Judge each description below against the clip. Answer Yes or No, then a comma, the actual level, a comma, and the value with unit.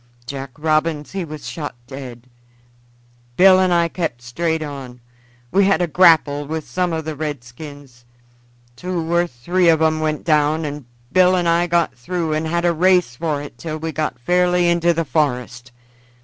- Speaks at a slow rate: No, average, 175 wpm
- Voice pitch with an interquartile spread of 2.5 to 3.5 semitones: Yes, average, 3.2 semitones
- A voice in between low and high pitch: Yes, medium, 160 Hz